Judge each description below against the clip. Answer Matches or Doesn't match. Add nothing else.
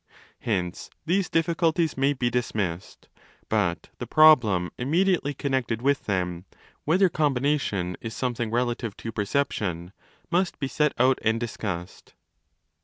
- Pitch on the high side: Doesn't match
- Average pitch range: Doesn't match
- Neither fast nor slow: Doesn't match